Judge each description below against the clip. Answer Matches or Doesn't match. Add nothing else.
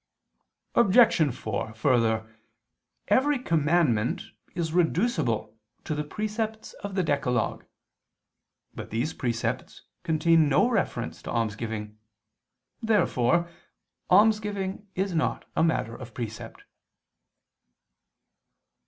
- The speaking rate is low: Matches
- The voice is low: Doesn't match